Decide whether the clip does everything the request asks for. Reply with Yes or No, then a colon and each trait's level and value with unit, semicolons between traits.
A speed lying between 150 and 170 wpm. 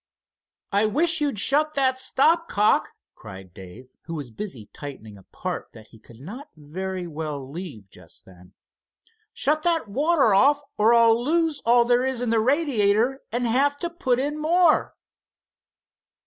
Yes: average, 160 wpm